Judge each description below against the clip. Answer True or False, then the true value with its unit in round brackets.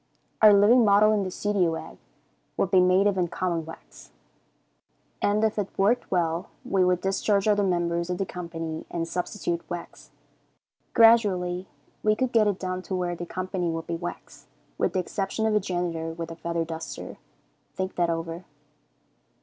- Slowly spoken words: False (170 wpm)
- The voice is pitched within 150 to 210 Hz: True (185 Hz)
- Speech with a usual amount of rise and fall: True (3.1 semitones)